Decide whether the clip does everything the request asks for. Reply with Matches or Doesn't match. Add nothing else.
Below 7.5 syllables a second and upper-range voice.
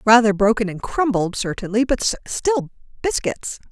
Matches